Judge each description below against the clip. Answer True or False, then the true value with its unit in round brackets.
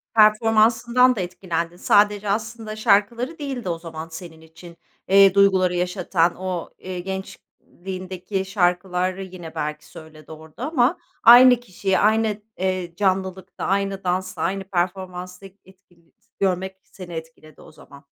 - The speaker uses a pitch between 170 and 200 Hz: True (185 Hz)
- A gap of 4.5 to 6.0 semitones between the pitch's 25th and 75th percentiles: False (2.8 semitones)